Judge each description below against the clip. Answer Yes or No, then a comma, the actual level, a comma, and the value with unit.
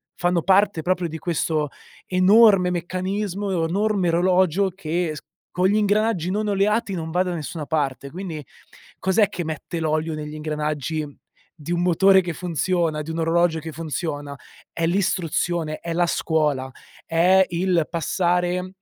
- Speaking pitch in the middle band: Yes, medium, 175 Hz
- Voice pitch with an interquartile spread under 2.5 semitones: No, average, 2.8 semitones